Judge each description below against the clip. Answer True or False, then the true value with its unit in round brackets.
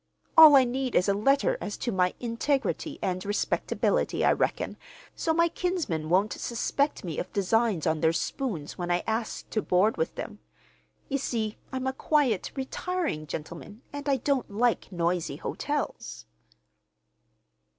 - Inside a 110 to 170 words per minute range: True (150 wpm)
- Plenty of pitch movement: True (7.2 semitones)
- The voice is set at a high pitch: True (225 Hz)